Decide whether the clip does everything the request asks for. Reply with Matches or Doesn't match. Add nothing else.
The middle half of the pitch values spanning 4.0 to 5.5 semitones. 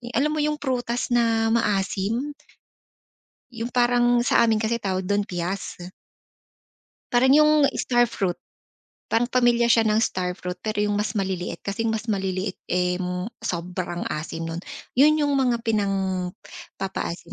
Matches